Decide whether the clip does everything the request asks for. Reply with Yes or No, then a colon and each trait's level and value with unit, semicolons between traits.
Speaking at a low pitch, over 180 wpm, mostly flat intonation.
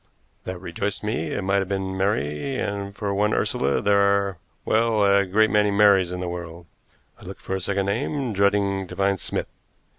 Yes: low, 100 Hz; average, 190 wpm; narrow, 1.5 semitones